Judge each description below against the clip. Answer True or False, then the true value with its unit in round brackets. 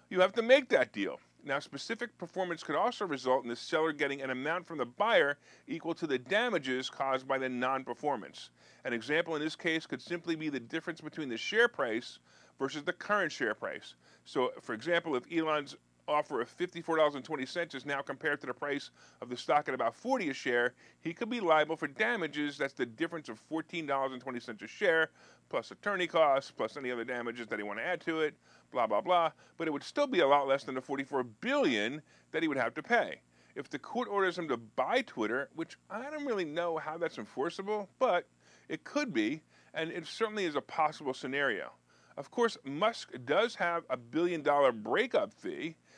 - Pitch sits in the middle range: True (155 Hz)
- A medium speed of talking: False (215 wpm)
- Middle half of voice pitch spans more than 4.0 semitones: True (4.7 semitones)